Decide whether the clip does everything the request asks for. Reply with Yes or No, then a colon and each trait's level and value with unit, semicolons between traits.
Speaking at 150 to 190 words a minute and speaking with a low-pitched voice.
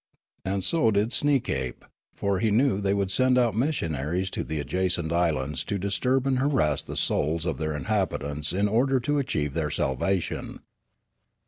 Yes: average, 180 wpm; very low, 95 Hz